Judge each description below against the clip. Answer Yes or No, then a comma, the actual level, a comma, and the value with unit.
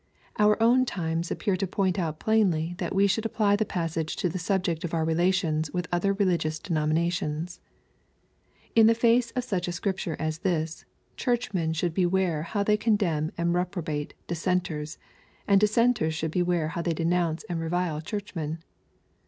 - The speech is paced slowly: No, average, 160 wpm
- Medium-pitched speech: Yes, medium, 175 Hz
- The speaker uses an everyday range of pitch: Yes, average, 3.8 semitones